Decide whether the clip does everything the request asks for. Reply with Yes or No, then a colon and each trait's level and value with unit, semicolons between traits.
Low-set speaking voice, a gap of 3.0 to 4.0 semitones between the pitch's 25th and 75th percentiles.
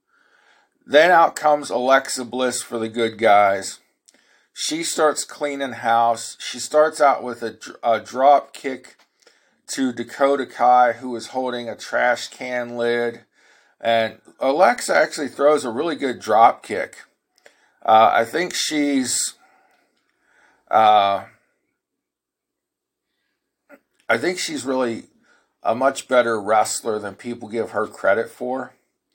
Yes: low, 125 Hz; average, 3.3 semitones